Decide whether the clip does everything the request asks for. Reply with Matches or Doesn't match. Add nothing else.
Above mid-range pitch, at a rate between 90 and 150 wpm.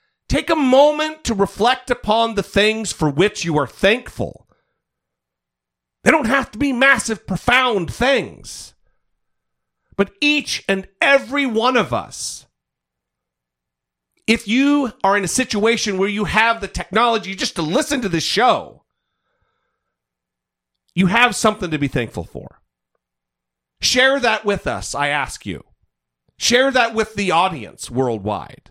Matches